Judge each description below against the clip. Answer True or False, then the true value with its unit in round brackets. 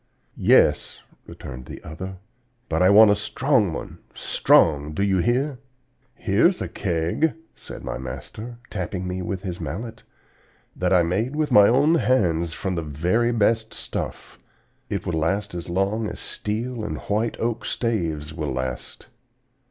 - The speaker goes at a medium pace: True (150 wpm)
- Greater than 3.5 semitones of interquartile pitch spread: True (5.3 semitones)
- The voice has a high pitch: False (100 Hz)